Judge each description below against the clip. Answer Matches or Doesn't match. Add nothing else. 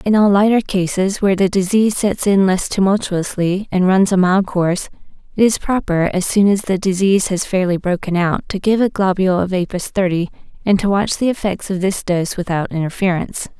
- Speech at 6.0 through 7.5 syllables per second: Doesn't match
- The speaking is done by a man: Doesn't match